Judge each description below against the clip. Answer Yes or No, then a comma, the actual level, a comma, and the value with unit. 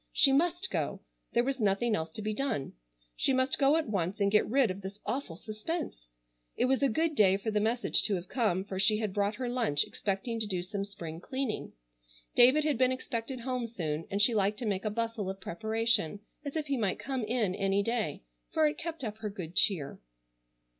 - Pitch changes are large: No, average, 4.8 semitones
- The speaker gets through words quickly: Yes, fast, 215 wpm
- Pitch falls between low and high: No, high, 215 Hz